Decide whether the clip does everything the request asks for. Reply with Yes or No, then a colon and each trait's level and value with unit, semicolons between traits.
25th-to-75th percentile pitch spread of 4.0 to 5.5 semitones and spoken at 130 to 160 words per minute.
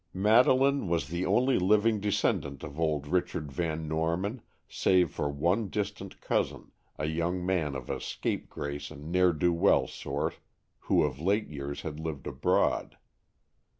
Yes: average, 4.5 semitones; average, 150 wpm